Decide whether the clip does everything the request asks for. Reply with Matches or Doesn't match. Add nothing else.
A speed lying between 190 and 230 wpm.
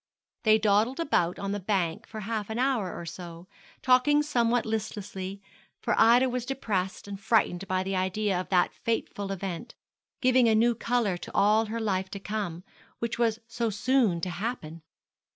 Doesn't match